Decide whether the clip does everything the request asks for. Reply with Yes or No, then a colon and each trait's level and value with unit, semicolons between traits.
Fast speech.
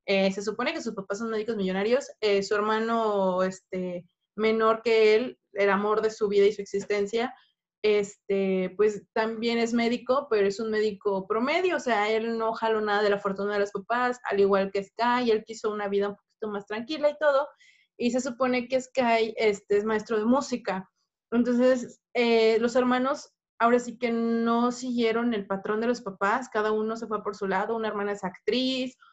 Yes: fast, 195 wpm